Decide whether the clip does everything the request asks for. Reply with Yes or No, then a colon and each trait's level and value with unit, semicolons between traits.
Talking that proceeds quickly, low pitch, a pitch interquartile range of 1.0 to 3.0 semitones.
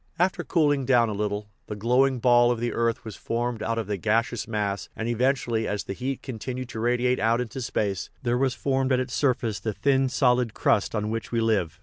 Yes: fast, 225 wpm; low, 120 Hz; narrow, 2.6 semitones